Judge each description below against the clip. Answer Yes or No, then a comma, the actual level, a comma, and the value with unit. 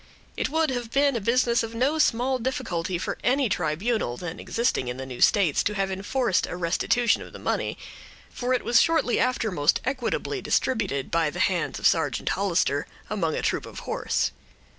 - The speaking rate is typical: Yes, average, 185 wpm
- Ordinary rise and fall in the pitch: No, wide, 6.9 semitones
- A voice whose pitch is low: No, high, 215 Hz